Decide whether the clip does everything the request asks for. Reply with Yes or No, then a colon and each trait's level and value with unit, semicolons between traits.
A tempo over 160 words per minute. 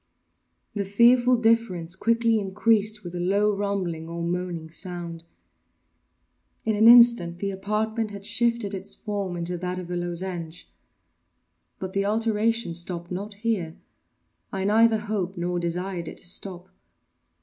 No: slow, 135 wpm